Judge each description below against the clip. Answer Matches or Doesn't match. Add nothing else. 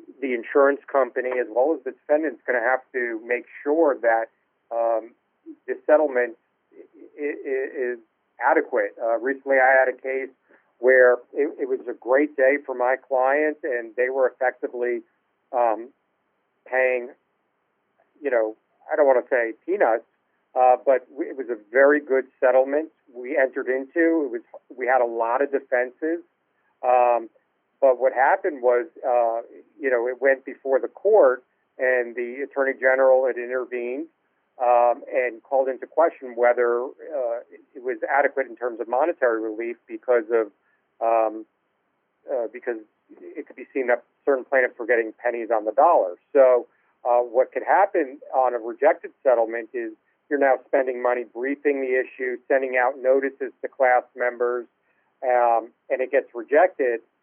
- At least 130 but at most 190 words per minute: Matches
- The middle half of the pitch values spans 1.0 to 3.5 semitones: Doesn't match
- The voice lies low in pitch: Matches